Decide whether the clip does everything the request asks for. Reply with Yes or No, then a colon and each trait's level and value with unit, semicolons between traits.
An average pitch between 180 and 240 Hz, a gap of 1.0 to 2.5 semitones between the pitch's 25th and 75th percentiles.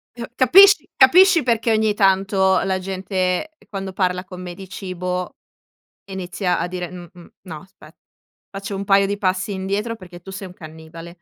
Yes: high, 190 Hz; narrow, 2.0 semitones